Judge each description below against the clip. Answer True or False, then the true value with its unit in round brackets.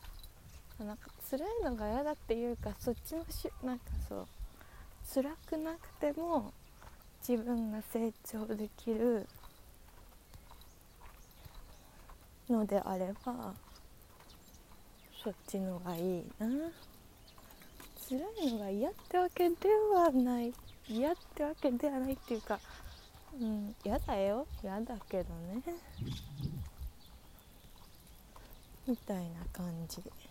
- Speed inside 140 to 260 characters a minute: True (190 characters per minute)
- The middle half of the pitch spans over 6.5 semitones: True (7.5 semitones)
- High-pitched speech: True (220 Hz)